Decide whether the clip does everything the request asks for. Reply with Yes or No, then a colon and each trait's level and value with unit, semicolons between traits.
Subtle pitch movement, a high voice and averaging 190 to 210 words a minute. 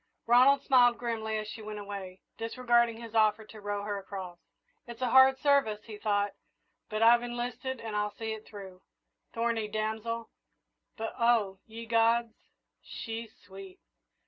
No: narrow, 2.3 semitones; high, 225 Hz; average, 150 wpm